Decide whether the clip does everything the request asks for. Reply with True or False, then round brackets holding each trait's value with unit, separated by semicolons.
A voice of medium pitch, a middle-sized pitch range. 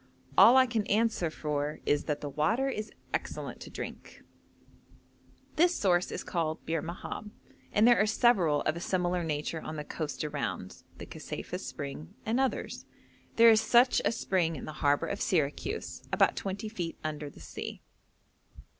False (175 Hz; 6.6 semitones)